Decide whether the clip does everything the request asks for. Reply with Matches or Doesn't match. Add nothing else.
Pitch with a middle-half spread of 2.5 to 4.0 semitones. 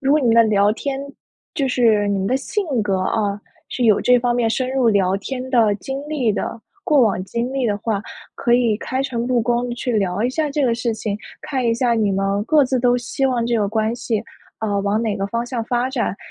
Matches